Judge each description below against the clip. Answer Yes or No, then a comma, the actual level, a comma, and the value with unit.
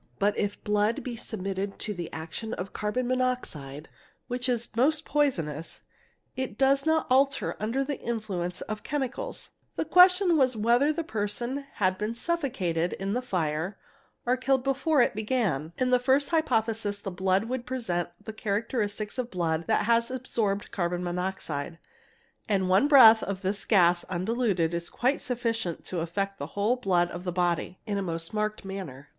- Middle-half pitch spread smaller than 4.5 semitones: No, wide, 5.6 semitones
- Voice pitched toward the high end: Yes, high, 215 Hz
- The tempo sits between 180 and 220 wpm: No, average, 165 wpm